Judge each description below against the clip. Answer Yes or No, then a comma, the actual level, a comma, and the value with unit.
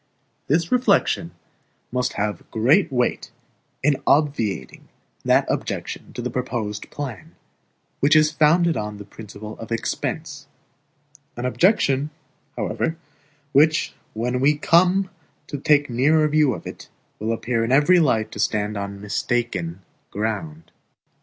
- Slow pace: Yes, slow, 130 wpm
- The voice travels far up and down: Yes, wide, 5.9 semitones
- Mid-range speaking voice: No, low, 130 Hz